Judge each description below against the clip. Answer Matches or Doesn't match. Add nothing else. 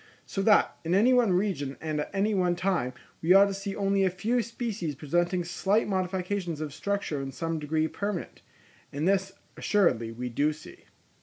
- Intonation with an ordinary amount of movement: Matches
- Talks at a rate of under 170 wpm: Doesn't match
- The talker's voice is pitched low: Doesn't match